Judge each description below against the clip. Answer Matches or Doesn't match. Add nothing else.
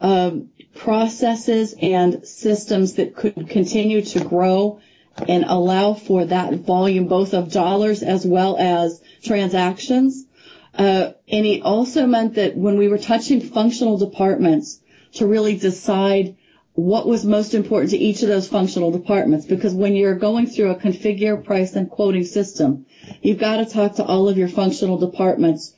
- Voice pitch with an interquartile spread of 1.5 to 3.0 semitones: Matches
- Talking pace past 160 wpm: Doesn't match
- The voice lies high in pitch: Matches